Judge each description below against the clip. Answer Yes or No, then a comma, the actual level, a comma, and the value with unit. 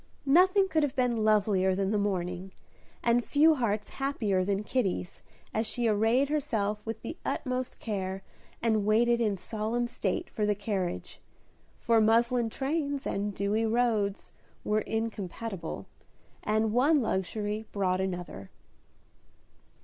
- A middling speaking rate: No, slow, 130 wpm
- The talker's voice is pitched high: Yes, high, 220 Hz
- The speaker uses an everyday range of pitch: Yes, average, 3.3 semitones